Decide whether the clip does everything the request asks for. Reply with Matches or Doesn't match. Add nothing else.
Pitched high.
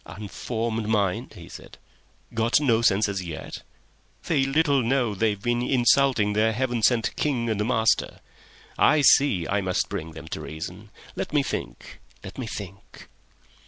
Doesn't match